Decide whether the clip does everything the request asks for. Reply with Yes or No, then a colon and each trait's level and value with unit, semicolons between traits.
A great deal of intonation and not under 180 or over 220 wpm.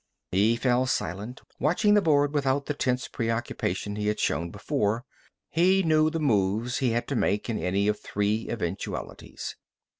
No: wide, 5.7 semitones; average, 160 wpm